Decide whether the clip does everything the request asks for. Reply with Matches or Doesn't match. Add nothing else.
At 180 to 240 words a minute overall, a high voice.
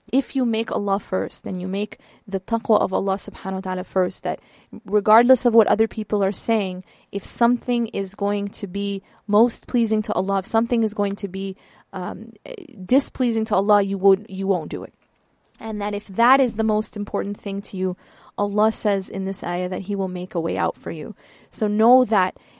Matches